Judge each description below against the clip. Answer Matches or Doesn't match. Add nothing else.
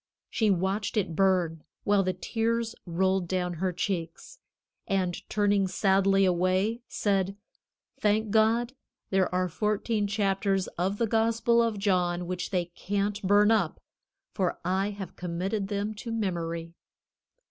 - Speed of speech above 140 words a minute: Doesn't match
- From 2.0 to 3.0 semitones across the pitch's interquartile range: Matches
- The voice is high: Matches